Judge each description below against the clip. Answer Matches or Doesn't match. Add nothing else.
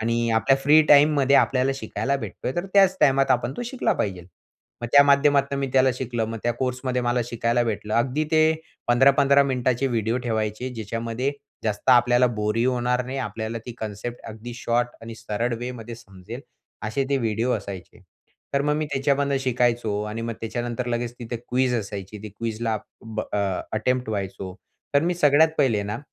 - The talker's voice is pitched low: Matches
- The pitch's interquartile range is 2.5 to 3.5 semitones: Matches